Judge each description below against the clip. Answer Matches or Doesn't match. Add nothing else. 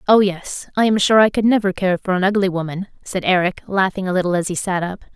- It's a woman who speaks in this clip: Matches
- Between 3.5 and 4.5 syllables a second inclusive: Doesn't match